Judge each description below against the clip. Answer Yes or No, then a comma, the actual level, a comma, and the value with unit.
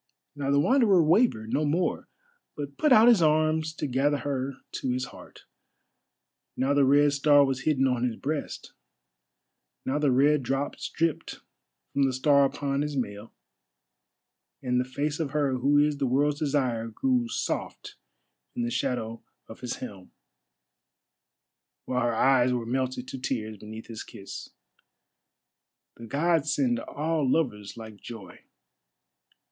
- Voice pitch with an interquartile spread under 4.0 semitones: Yes, average, 3.1 semitones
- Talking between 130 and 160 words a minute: Yes, average, 145 wpm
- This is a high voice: No, medium, 140 Hz